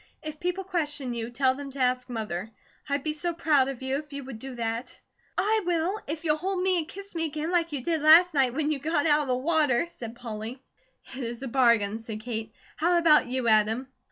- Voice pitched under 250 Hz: No, very high, 280 Hz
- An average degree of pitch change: Yes, average, 5.0 semitones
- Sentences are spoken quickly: Yes, fast, 230 wpm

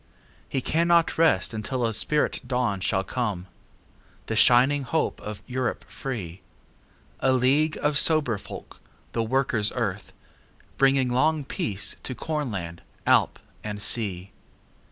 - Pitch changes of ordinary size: Yes, average, 5.0 semitones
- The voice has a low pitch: Yes, low, 125 Hz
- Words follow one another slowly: Yes, slow, 110 wpm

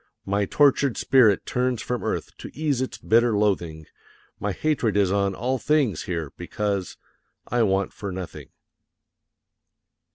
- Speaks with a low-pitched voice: Yes, low, 105 Hz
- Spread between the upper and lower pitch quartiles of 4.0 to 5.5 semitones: Yes, average, 4.6 semitones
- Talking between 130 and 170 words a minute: Yes, slow, 135 wpm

